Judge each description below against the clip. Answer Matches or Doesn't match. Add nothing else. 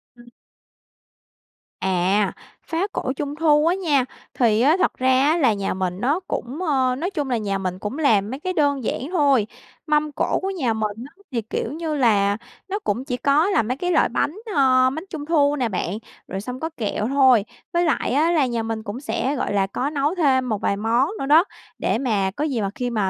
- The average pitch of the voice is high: Matches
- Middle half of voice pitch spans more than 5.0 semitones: Matches